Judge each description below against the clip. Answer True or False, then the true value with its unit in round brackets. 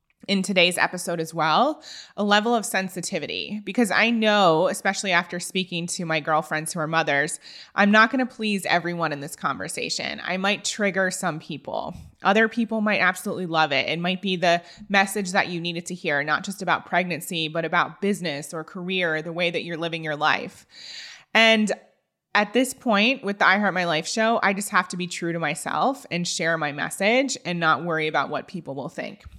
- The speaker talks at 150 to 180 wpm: False (200 wpm)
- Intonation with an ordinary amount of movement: True (3.5 semitones)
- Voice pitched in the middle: True (180 Hz)